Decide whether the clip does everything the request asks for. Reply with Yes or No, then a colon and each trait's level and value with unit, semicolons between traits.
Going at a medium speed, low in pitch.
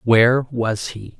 Yes: average, 150 wpm; low, 115 Hz